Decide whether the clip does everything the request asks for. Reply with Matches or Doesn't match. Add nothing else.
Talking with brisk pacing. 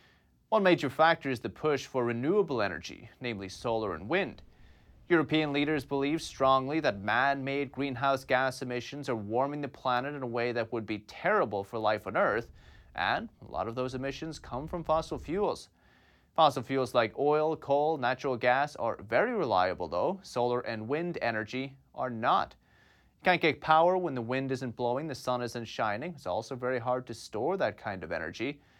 Doesn't match